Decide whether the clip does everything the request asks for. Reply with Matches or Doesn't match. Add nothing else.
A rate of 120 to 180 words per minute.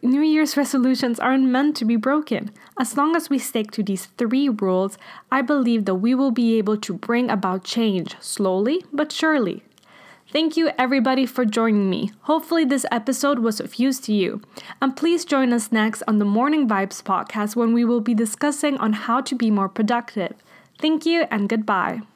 Doesn't match